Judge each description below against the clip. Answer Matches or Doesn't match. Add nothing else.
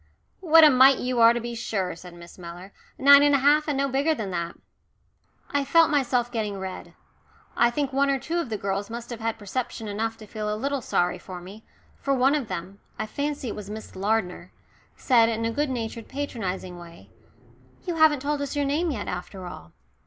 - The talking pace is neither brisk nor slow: Doesn't match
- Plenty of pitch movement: Matches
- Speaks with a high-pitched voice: Matches